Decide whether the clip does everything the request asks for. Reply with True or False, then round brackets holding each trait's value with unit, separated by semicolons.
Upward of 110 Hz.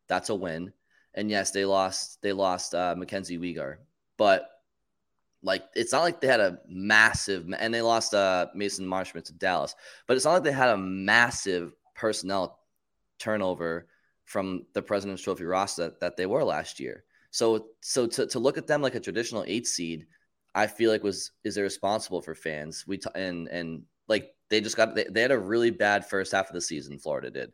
False (95 Hz)